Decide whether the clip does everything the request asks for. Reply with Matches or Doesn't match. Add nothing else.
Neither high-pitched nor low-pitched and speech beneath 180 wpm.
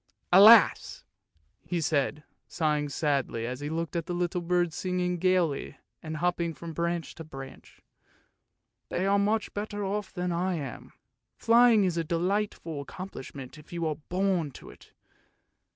Matches